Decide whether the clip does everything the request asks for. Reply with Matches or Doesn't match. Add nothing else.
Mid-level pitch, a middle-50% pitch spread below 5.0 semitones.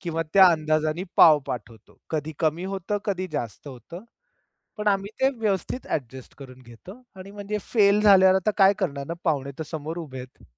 Doesn't match